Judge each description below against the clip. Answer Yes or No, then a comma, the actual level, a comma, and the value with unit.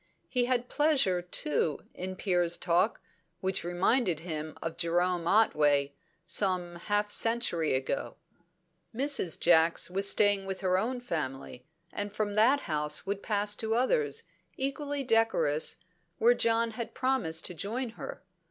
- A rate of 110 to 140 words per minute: Yes, slow, 135 wpm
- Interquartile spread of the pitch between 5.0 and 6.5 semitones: Yes, wide, 5.4 semitones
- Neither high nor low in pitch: No, high, 195 Hz